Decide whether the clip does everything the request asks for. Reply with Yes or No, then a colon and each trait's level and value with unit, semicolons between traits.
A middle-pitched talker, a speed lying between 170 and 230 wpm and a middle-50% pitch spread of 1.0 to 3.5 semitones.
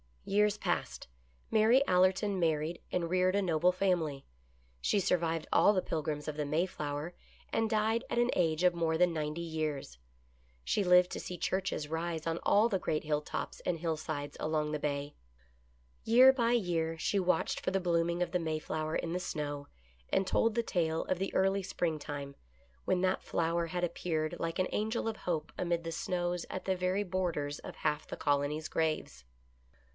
Yes: medium, 170 Hz; average, 180 wpm; average, 3.1 semitones